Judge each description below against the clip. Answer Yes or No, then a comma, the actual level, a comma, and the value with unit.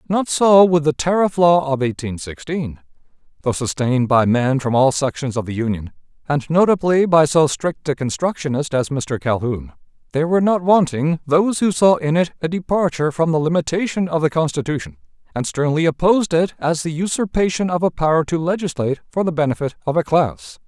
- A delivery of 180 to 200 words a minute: Yes, average, 185 wpm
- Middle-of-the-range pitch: Yes, medium, 150 Hz